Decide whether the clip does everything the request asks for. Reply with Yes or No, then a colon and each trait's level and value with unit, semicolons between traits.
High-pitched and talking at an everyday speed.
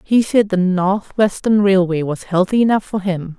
Yes: high, 195 Hz; average, 175 wpm